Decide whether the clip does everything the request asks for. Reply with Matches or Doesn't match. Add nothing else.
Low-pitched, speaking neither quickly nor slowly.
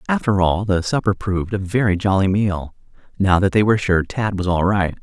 Doesn't match